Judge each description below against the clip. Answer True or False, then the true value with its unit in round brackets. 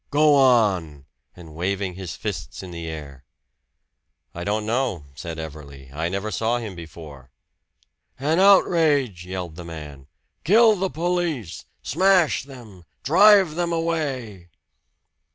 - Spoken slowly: True (125 wpm)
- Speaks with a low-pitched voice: True (105 Hz)